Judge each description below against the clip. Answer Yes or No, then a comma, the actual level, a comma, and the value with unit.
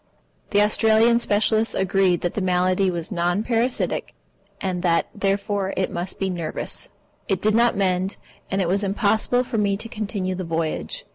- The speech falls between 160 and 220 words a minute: Yes, average, 165 wpm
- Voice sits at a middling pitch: No, high, 195 Hz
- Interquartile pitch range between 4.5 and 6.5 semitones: No, average, 2.8 semitones